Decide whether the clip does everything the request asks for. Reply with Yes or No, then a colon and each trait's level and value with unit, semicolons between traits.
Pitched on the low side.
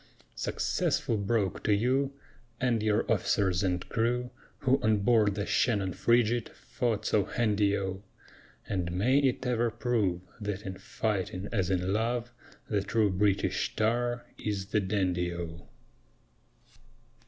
Yes: low, 105 Hz